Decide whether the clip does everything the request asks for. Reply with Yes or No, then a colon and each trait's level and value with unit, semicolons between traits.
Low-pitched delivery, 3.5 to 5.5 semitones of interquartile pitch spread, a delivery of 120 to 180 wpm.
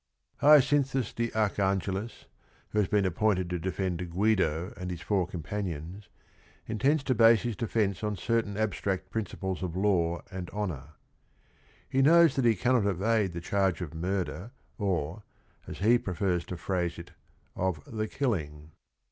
Yes: low, 100 Hz; average, 4.0 semitones; average, 175 wpm